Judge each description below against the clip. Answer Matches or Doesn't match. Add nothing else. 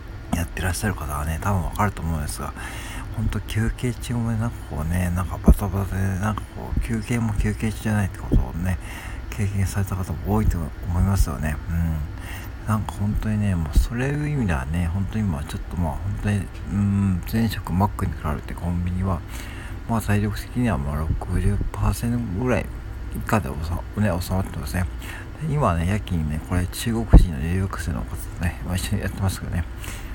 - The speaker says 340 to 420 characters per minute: Matches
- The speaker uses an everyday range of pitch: Matches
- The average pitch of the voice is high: Doesn't match